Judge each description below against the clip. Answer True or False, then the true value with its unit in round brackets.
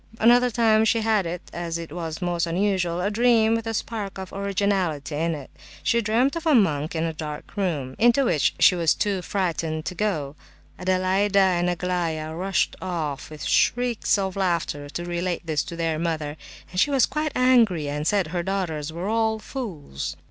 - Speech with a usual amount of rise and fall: True (4.7 semitones)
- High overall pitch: False (180 Hz)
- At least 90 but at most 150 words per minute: False (175 wpm)